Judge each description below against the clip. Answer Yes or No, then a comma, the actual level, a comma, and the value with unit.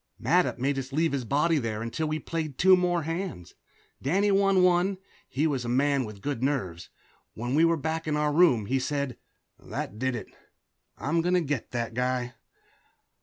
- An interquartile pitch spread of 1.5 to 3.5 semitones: No, average, 5.0 semitones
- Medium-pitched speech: Yes, medium, 145 Hz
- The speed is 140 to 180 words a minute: No, average, 190 wpm